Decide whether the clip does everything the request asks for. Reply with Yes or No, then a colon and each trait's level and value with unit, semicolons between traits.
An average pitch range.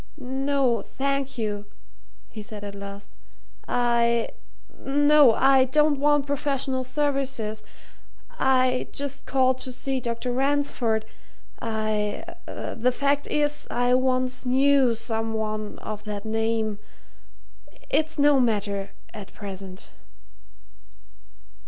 Yes: average, 4.0 semitones